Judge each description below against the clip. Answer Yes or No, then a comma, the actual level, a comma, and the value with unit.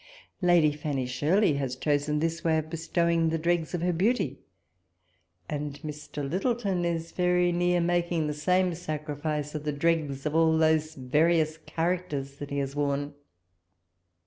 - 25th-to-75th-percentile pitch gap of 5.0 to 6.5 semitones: No, average, 2.8 semitones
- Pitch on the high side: No, medium, 160 Hz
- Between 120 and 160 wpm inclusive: Yes, average, 155 wpm